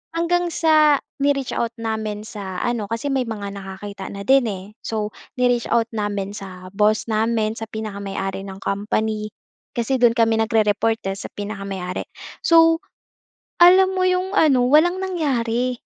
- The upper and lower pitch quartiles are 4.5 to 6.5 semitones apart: Yes, average, 4.8 semitones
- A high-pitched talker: Yes, high, 225 Hz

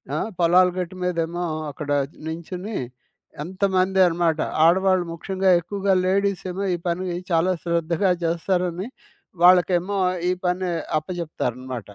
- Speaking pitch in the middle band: Yes, medium, 180 Hz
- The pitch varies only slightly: Yes, narrow, 2.1 semitones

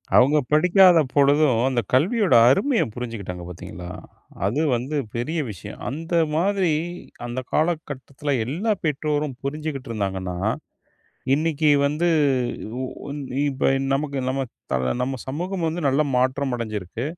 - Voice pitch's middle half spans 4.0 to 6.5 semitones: Yes, average, 4.4 semitones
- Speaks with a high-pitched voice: No, medium, 140 Hz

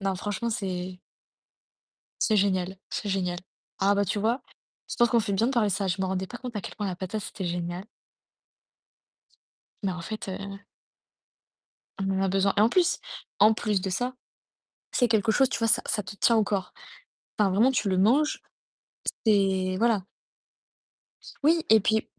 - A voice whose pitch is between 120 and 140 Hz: No, high, 200 Hz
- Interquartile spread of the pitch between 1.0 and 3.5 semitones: Yes, average, 2.8 semitones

